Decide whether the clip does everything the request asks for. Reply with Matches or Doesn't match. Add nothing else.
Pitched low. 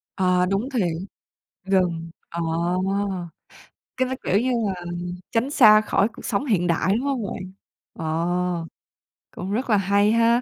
Doesn't match